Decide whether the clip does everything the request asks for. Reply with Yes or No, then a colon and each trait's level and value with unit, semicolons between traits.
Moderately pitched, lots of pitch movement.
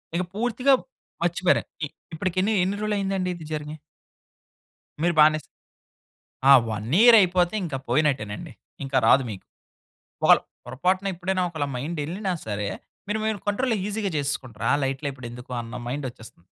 Yes: medium, 165 Hz; wide, 6.5 semitones